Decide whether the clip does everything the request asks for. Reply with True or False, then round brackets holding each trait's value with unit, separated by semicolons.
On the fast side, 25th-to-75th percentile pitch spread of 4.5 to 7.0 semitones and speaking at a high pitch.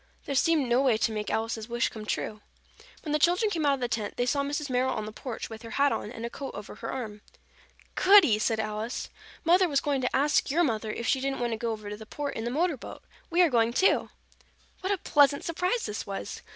True (250 wpm; 5.0 semitones; 255 Hz)